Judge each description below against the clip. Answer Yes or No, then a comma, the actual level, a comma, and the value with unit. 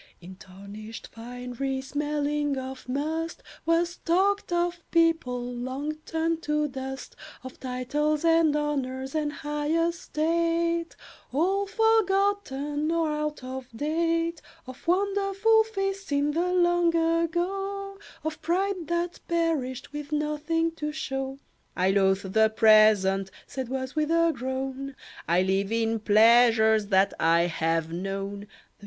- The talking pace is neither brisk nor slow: No, slow, 125 wpm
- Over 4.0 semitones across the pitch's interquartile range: Yes, average, 5.2 semitones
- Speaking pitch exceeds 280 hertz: Yes, very high, 295 Hz